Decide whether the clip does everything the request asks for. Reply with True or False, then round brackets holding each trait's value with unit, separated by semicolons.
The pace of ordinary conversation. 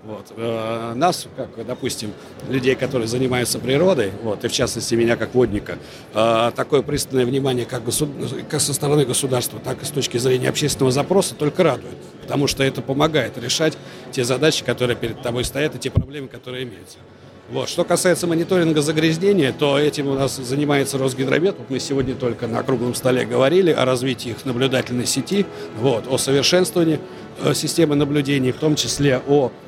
False (165 wpm)